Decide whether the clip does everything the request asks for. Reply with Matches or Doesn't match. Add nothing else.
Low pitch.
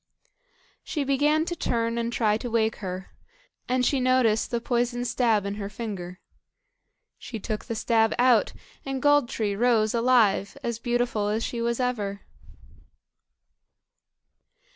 Doesn't match